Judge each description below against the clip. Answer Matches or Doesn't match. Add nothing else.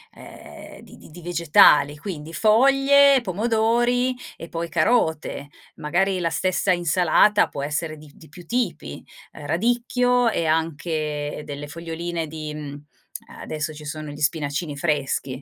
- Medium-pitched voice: Matches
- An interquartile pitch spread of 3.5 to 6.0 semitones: Matches